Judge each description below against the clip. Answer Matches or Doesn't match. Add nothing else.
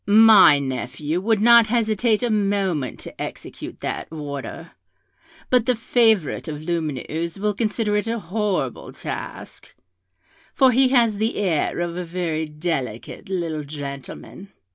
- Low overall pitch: Doesn't match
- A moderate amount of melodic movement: Doesn't match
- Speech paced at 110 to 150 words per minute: Matches